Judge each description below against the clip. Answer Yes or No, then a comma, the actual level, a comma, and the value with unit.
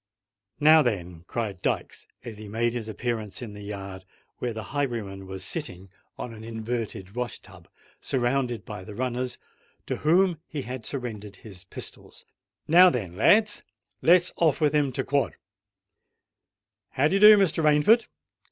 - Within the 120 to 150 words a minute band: Yes, average, 145 wpm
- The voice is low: Yes, low, 120 Hz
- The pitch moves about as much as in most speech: No, wide, 6.1 semitones